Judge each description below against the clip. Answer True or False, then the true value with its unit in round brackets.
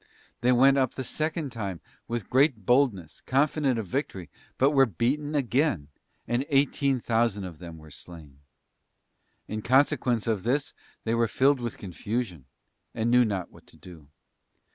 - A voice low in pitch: True (120 Hz)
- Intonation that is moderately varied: False (5.9 semitones)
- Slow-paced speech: False (155 wpm)